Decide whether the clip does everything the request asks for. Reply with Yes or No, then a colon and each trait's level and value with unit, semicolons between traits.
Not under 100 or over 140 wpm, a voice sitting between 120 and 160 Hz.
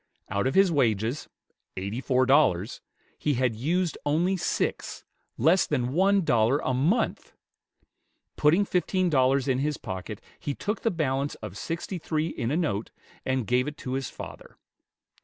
No: average, 160 wpm; medium, 140 Hz